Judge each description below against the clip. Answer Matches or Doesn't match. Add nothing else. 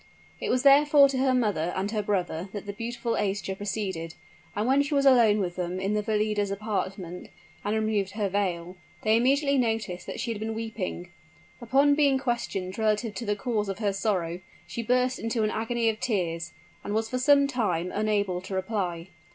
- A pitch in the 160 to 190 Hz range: Doesn't match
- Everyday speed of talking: Matches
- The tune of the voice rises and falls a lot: Doesn't match